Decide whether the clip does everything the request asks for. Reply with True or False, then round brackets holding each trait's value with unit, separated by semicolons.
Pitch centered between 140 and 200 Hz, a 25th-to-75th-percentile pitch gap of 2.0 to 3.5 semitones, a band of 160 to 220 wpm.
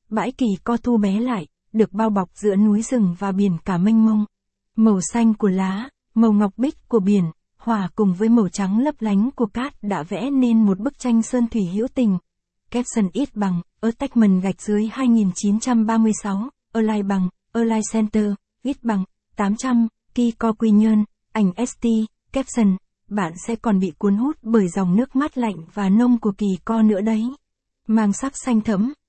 False (220 Hz; 2.6 semitones; 190 wpm)